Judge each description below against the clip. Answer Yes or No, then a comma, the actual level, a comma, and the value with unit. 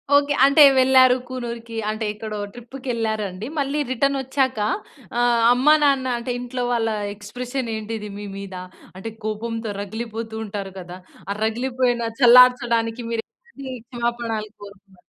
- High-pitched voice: Yes, high, 235 Hz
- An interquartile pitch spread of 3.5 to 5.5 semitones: No, average, 2.8 semitones